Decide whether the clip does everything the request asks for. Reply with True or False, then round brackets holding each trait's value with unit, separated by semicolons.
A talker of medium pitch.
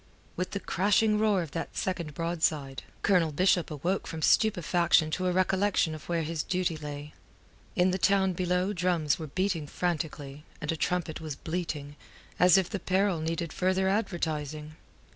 True (175 Hz)